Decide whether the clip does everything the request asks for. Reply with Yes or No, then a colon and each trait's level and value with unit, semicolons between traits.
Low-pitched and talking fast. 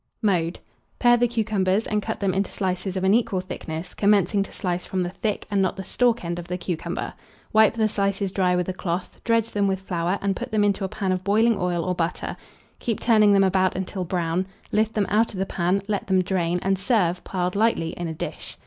No: high, 190 Hz; fast, 230 wpm